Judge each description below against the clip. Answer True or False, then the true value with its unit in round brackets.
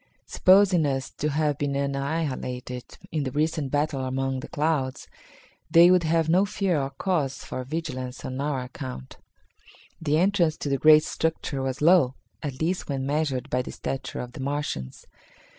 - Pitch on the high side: False (145 Hz)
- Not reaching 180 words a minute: True (165 wpm)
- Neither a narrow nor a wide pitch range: True (3.4 semitones)